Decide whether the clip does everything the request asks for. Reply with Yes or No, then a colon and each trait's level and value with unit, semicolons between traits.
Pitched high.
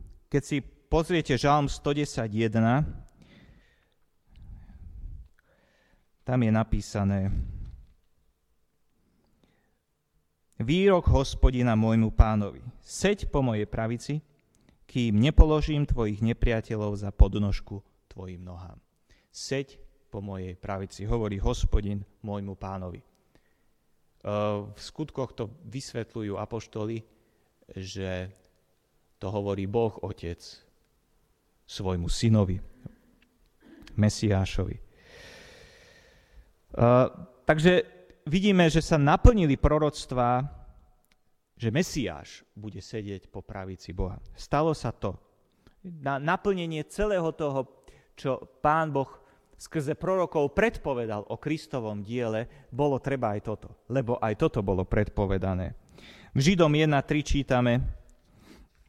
No: low, 110 Hz